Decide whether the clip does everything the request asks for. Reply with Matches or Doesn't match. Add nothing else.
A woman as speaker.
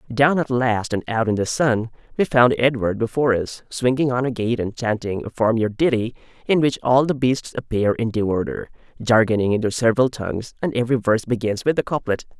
Doesn't match